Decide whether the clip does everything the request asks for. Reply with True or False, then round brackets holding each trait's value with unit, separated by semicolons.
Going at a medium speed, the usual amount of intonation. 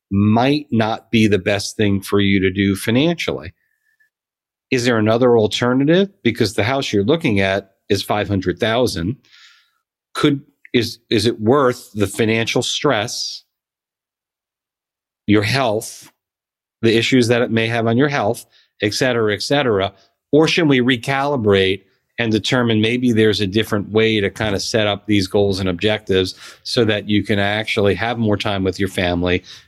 True (160 wpm; 3.6 semitones)